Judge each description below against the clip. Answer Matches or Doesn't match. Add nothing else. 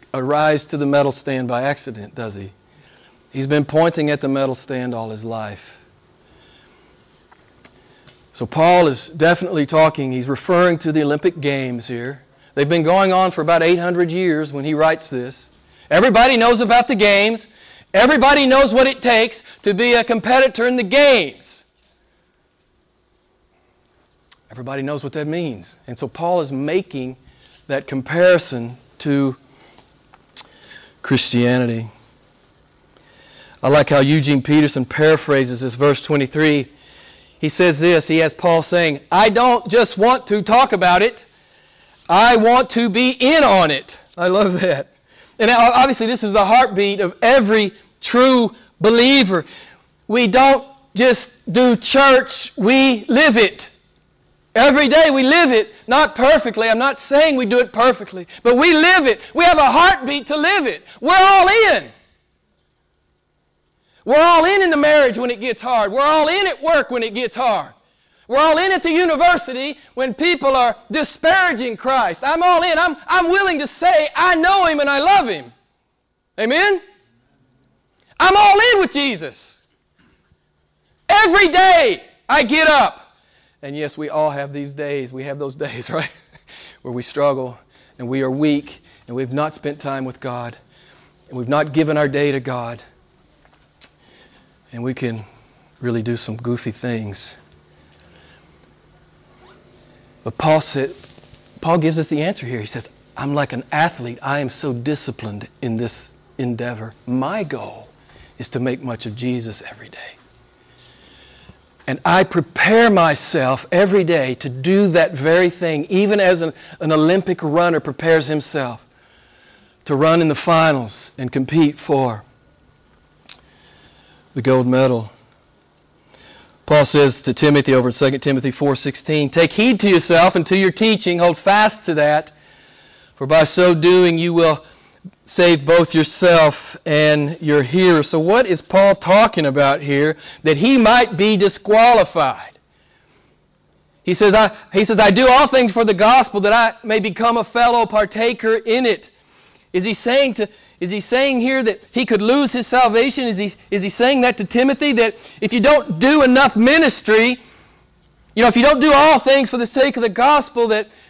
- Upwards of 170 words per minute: Doesn't match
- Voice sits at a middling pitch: Matches